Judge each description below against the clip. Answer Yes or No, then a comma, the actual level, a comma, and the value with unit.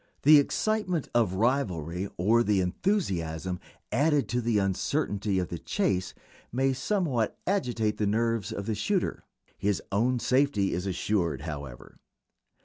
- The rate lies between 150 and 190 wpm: No, slow, 135 wpm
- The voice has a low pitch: Yes, low, 110 Hz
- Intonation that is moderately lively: No, wide, 6.3 semitones